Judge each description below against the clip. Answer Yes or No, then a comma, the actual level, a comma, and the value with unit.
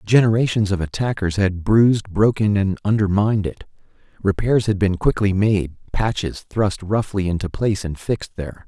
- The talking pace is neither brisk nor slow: Yes, average, 150 wpm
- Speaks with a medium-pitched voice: No, low, 100 Hz